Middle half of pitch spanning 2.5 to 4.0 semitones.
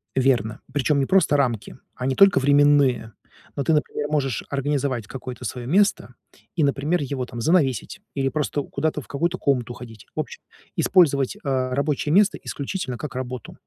Yes: average, 2.8 semitones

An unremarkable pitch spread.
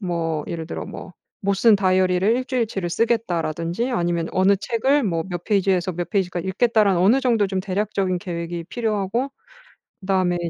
Yes: average, 3.7 semitones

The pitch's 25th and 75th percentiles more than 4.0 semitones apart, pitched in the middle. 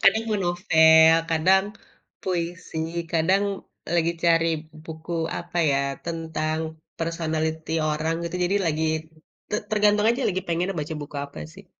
No: narrow, 2.6 semitones; medium, 165 Hz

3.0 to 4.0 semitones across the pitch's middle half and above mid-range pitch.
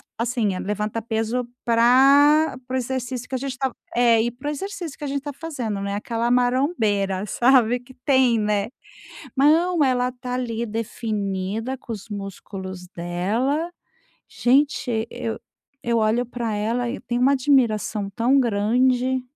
Yes: average, 3.4 semitones; high, 240 Hz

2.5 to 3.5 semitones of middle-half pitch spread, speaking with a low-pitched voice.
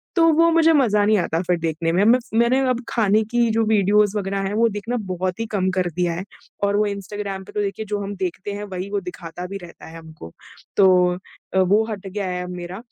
No: average, 3.0 semitones; high, 200 Hz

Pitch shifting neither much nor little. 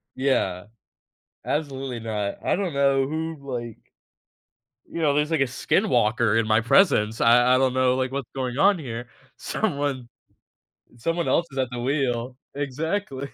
Yes: average, 3.3 semitones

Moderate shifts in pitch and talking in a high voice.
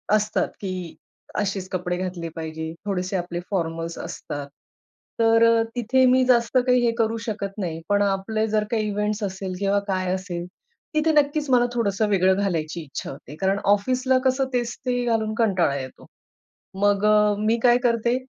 Yes: average, 4.0 semitones; high, 205 Hz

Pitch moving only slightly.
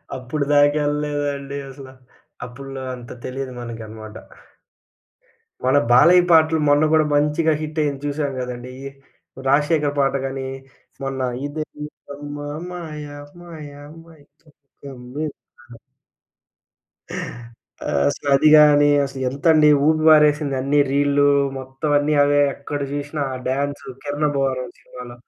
Yes: narrow, 2.1 semitones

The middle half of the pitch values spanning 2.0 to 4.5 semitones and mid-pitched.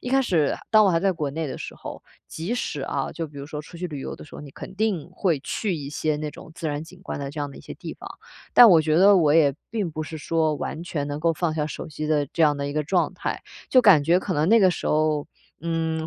Yes: average, 3.4 semitones; medium, 160 Hz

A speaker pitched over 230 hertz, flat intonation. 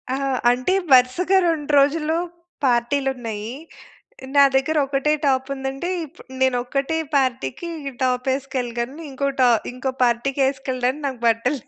Yes: very high, 265 Hz; narrow, 2.2 semitones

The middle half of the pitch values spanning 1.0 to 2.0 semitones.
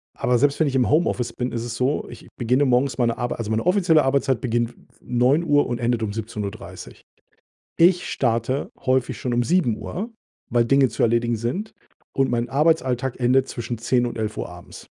No: average, 2.9 semitones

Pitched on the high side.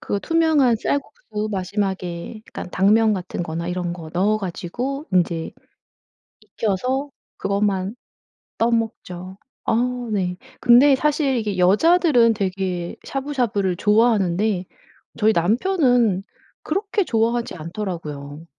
Yes: high, 210 Hz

